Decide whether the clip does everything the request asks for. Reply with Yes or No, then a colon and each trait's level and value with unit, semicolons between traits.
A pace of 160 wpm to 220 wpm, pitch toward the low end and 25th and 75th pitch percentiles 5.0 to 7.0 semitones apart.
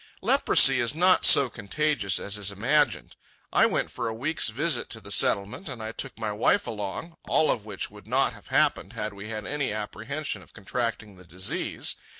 Yes: average, 185 wpm; low, 110 Hz; wide, 5.5 semitones